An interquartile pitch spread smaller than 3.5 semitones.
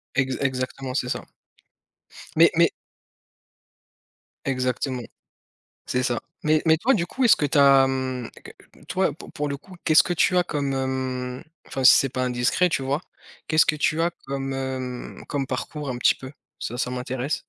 Yes: average, 2.9 semitones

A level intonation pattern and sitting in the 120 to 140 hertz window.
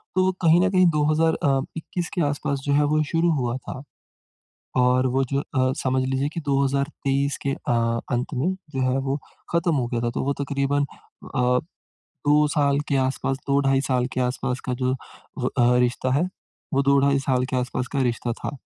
Yes: narrow, 2.1 semitones; low, 135 Hz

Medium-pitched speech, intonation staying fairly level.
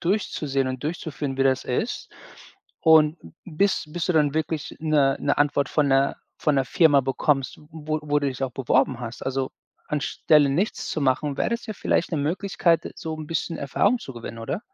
No: medium, 145 Hz; average, 3.1 semitones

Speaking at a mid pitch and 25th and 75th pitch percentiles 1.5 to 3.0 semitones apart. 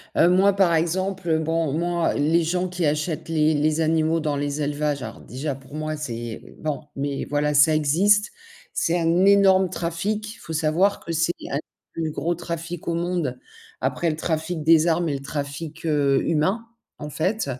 Yes: medium, 160 Hz; average, 2.7 semitones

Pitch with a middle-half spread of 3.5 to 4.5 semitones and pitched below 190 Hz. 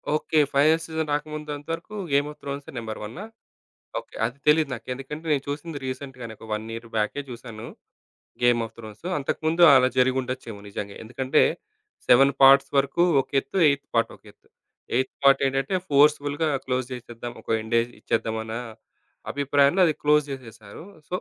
Yes: average, 3.9 semitones; low, 135 Hz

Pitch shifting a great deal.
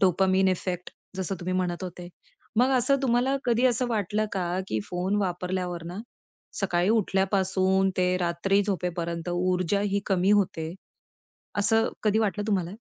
No: narrow, 2.5 semitones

